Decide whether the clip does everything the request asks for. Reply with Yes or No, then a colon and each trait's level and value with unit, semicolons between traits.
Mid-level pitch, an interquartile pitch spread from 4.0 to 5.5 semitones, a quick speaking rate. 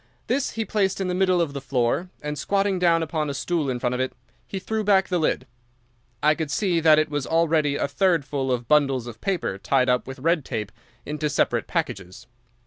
Yes: medium, 155 Hz; average, 5.1 semitones; fast, 220 wpm